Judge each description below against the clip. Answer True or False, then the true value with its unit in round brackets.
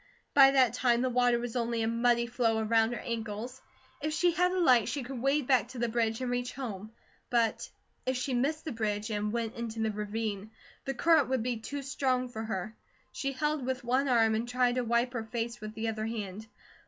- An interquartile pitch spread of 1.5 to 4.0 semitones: True (2.5 semitones)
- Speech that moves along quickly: True (220 wpm)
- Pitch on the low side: False (240 Hz)